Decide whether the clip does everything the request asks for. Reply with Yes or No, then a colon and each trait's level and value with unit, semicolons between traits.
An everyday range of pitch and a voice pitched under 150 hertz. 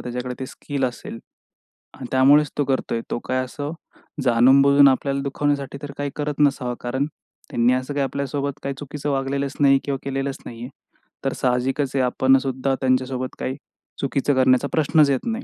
No: narrow, 1.6 semitones; low, 135 Hz